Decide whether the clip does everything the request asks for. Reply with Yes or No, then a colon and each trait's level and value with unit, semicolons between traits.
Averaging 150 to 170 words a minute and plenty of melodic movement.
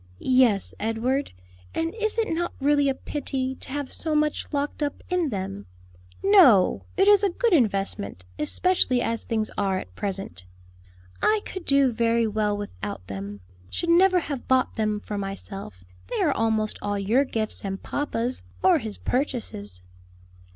Yes: average, 160 wpm; wide, 6.7 semitones